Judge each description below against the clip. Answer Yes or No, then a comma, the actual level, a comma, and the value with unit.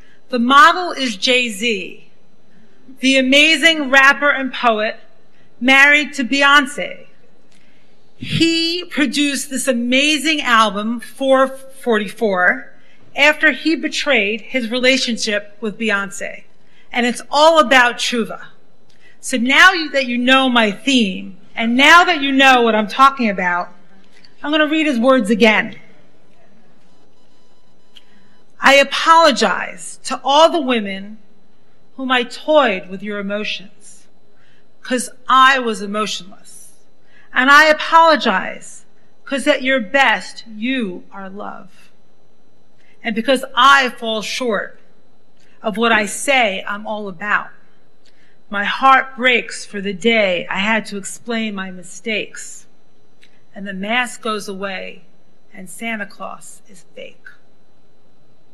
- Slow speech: Yes, slow, 115 wpm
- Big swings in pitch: No, average, 4.6 semitones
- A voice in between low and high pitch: No, high, 245 Hz